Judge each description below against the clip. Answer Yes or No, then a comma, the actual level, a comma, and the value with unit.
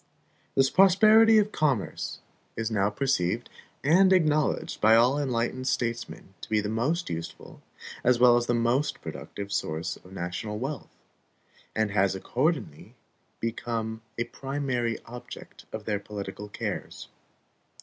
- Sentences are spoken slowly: Yes, slow, 130 wpm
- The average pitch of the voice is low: Yes, low, 120 Hz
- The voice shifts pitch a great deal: No, average, 5.0 semitones